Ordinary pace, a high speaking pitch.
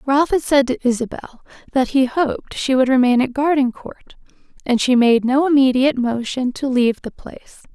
Yes: average, 180 wpm; very high, 260 Hz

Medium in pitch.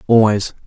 No: low, 110 Hz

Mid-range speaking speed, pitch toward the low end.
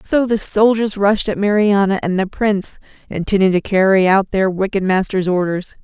No: average, 175 wpm; high, 195 Hz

